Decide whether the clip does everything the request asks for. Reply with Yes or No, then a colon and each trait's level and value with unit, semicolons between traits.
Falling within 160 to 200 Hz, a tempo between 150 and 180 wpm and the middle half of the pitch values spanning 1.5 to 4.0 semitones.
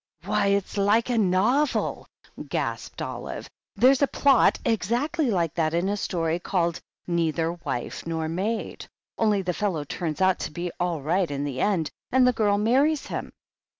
No: high, 190 Hz; average, 170 wpm; average, 5.3 semitones